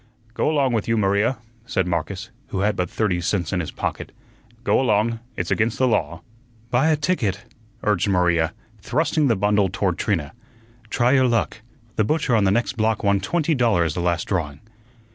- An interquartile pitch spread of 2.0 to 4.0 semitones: No, average, 4.7 semitones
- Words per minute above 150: Yes, average, 180 wpm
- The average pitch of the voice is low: Yes, low, 105 Hz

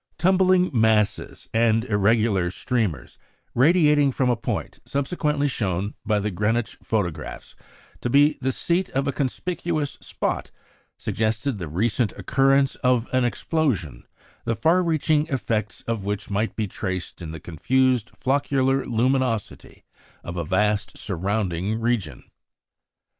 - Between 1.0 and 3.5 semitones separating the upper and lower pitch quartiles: No, average, 5.0 semitones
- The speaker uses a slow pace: Yes, slow, 125 wpm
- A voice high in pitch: No, low, 115 Hz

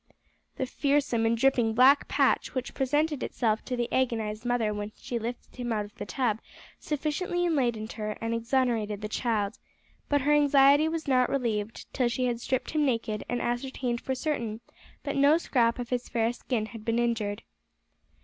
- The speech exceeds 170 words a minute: Yes, average, 180 wpm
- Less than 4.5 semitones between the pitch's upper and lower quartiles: Yes, average, 3.3 semitones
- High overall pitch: Yes, high, 245 Hz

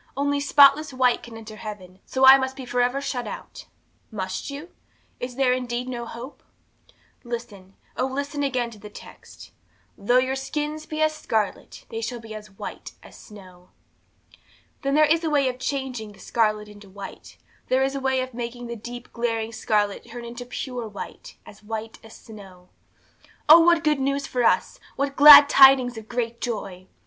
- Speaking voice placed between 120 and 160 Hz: No, high, 245 Hz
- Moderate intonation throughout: Yes, average, 3.8 semitones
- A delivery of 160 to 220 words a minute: Yes, average, 180 wpm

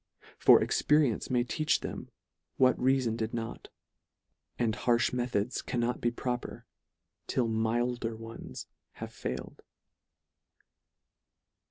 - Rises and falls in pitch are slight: Yes, narrow, 1.7 semitones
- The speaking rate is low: Yes, slow, 105 wpm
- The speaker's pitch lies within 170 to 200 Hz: No, low, 120 Hz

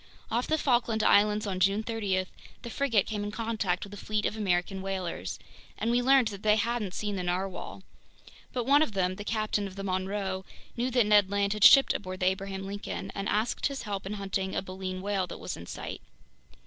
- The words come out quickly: Yes, fast, 210 wpm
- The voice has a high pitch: Yes, high, 205 Hz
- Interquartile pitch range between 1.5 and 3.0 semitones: Yes, narrow, 2.5 semitones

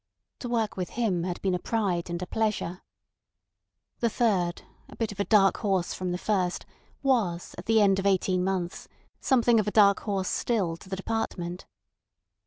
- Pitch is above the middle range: Yes, high, 195 Hz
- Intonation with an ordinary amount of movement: Yes, average, 3.5 semitones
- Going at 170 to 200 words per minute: Yes, average, 185 wpm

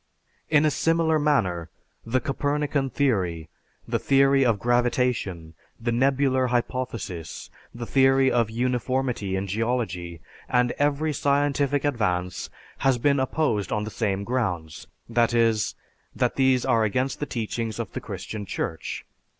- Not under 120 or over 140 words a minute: Yes, slow, 135 wpm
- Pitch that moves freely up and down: No, average, 4.4 semitones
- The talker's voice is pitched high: No, low, 125 Hz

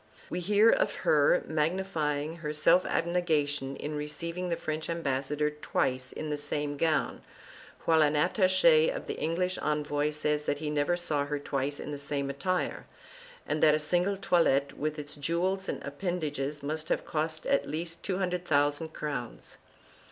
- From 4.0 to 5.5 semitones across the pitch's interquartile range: No, average, 3.2 semitones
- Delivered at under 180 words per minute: Yes, average, 160 wpm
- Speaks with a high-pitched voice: No, medium, 155 Hz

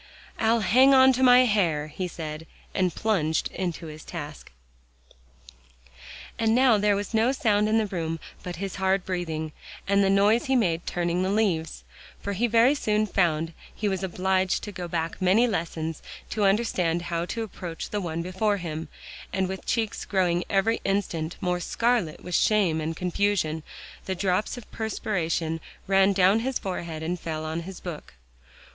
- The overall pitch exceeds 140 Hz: Yes, high, 190 Hz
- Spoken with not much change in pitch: No, average, 4.2 semitones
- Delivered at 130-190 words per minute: Yes, average, 170 wpm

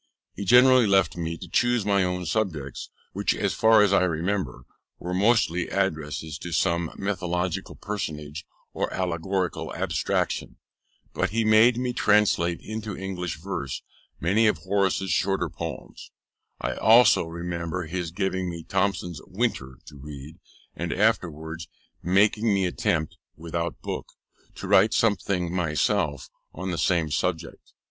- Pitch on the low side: Yes, very low, 90 Hz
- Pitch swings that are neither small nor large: Yes, average, 3.5 semitones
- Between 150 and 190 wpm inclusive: No, slow, 135 wpm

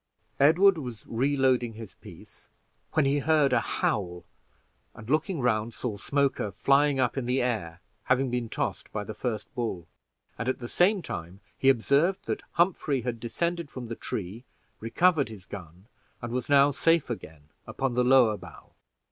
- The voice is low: Yes, low, 125 Hz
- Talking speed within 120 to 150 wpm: No, average, 165 wpm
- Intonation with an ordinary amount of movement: Yes, average, 4.4 semitones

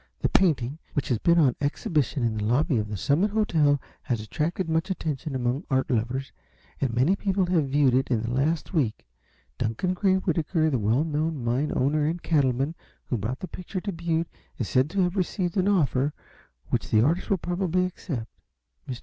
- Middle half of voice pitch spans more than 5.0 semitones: Yes, wide, 5.5 semitones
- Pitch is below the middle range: No, medium, 150 Hz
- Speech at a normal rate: Yes, average, 190 wpm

